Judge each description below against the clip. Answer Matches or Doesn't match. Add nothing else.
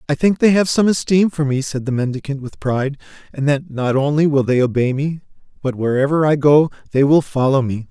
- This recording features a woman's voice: Doesn't match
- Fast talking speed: Matches